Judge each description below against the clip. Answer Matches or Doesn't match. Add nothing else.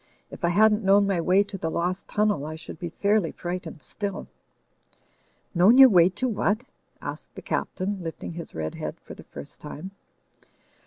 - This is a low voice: Doesn't match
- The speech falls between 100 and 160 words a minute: Doesn't match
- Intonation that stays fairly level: Doesn't match